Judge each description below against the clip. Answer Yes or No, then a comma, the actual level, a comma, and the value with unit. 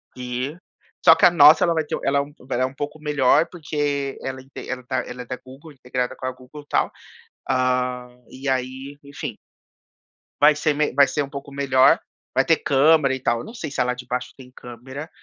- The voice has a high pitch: No, low, 135 Hz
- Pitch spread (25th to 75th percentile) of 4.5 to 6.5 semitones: No, narrow, 2.5 semitones